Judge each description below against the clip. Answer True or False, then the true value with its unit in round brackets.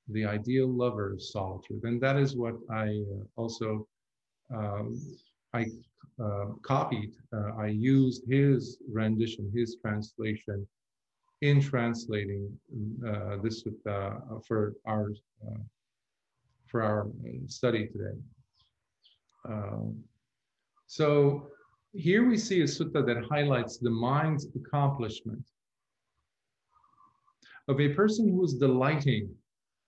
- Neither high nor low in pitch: False (115 Hz)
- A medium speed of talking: False (100 wpm)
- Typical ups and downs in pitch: True (3.7 semitones)